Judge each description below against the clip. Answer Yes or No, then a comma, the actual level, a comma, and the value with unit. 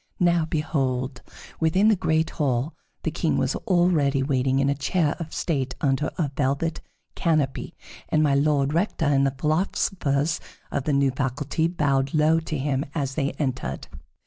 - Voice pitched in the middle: Yes, medium, 145 Hz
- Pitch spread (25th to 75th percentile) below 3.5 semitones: Yes, average, 2.8 semitones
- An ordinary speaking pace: Yes, average, 160 wpm